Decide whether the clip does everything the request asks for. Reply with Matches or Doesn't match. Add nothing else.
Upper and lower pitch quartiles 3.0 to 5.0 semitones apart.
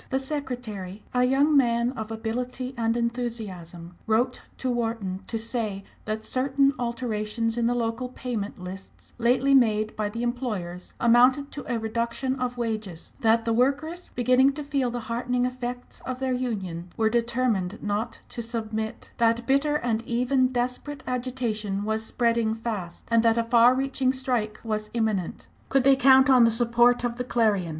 Doesn't match